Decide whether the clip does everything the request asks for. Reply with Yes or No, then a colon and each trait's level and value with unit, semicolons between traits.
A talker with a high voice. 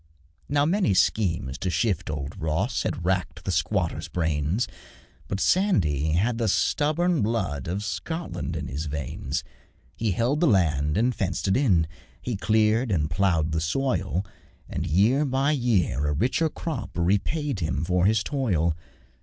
No: very low, 95 Hz